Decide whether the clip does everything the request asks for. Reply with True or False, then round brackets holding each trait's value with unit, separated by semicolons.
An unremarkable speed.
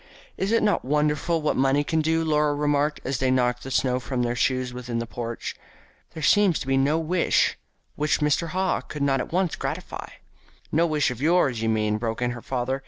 False (210 wpm)